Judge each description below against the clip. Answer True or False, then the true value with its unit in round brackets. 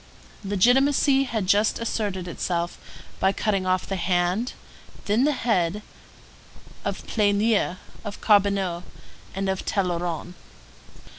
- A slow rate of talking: True (105 wpm)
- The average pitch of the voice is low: False (200 Hz)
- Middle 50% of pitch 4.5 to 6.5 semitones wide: False (3.3 semitones)